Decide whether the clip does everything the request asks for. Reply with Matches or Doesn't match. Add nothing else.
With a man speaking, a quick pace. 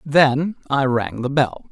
Doesn't match